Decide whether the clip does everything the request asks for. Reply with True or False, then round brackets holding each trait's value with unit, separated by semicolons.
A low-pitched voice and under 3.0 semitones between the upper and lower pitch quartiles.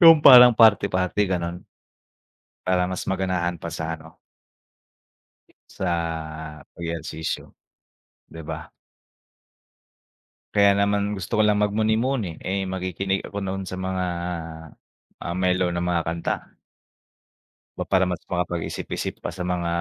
True (95 Hz; 2.6 semitones)